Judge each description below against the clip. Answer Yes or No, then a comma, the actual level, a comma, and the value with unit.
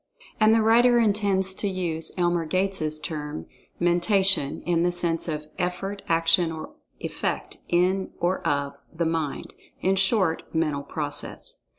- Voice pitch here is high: No, medium, 175 Hz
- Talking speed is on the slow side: Yes, slow, 130 wpm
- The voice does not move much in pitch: No, average, 3.1 semitones